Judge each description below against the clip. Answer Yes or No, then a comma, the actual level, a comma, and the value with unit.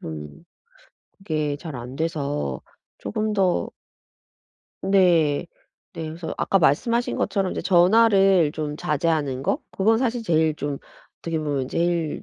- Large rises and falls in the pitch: No, average, 4.7 semitones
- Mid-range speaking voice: Yes, medium, 165 Hz